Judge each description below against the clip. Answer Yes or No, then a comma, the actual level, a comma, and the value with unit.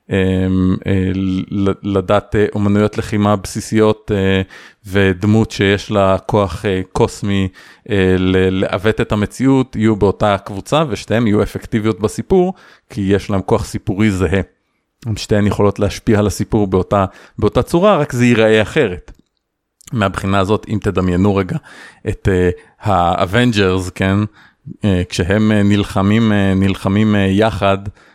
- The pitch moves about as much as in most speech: No, narrow, 2.0 semitones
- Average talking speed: Yes, average, 125 wpm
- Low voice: Yes, low, 100 Hz